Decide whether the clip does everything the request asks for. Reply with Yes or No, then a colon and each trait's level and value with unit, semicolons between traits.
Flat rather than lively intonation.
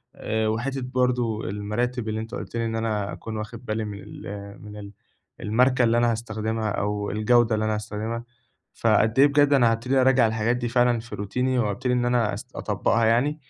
Yes: narrow, 2.3 semitones